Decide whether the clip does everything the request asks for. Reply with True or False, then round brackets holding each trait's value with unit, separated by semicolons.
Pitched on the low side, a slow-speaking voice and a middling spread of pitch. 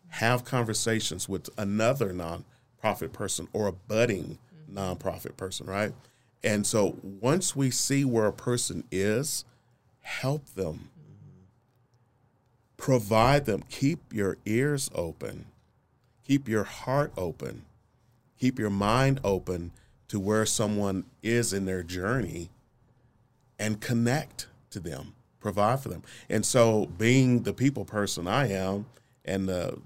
True (115 Hz; 125 wpm; 4.2 semitones)